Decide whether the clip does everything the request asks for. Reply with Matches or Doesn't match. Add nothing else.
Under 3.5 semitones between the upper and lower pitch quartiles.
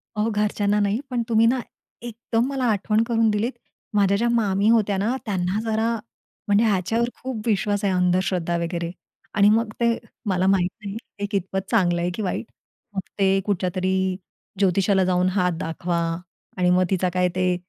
Matches